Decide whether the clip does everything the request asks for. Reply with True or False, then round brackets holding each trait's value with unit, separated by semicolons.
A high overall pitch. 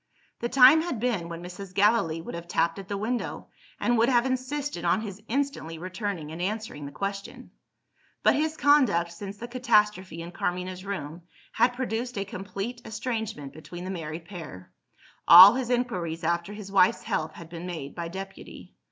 True (195 Hz)